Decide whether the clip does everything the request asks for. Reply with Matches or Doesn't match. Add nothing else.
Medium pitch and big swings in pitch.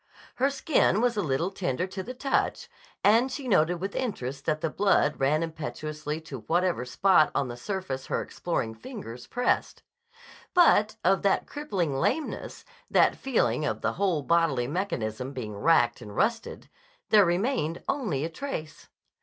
Matches